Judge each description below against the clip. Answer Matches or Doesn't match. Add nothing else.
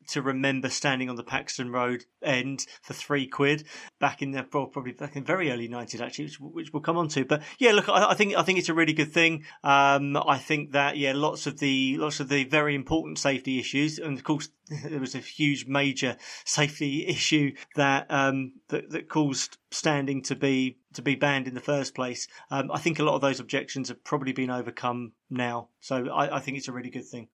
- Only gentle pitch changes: Matches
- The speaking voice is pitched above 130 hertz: Matches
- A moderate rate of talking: Doesn't match